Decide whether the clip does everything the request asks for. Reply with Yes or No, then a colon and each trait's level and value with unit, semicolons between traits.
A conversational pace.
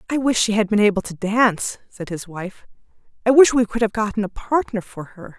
No: fast, 235 wpm